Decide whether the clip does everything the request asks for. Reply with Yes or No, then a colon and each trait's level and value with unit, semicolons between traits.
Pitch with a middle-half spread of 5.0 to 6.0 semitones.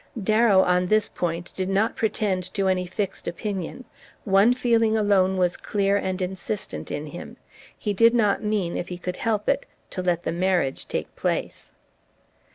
No: average, 2.9 semitones